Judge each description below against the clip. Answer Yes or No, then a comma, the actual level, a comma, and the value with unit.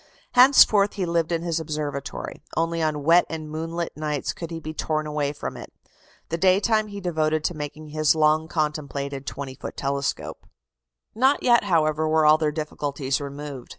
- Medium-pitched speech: Yes, medium, 155 Hz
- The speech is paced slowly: No, average, 175 wpm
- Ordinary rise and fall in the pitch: No, narrow, 2.1 semitones